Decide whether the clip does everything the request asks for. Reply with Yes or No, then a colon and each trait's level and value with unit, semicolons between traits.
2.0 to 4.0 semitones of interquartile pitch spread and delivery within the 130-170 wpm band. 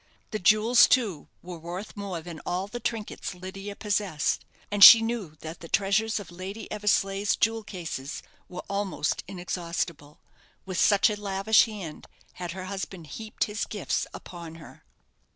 Yes: average, 3.2 semitones; average, 150 wpm